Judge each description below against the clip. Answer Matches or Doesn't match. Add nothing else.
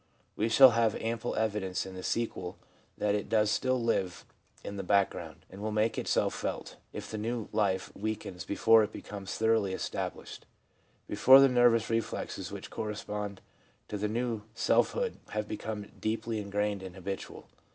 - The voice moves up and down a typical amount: Doesn't match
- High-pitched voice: Doesn't match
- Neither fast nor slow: Matches